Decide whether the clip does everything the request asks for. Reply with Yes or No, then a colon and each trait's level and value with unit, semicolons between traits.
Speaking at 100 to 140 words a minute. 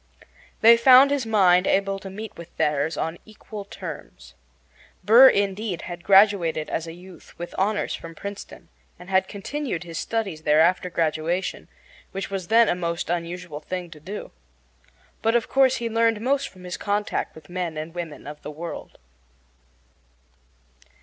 No: average, 160 wpm